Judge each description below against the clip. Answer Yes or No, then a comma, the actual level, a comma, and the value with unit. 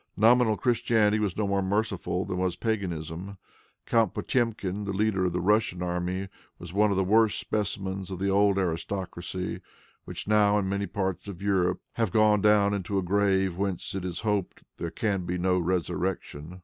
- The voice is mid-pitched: No, very low, 95 Hz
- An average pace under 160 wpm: No, average, 185 wpm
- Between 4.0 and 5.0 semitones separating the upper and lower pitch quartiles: No, narrow, 2.4 semitones